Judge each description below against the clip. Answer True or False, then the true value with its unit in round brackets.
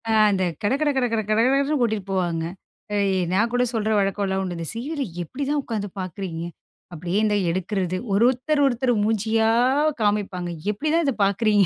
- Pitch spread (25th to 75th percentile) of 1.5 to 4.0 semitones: False (4.5 semitones)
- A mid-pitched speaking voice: False (210 Hz)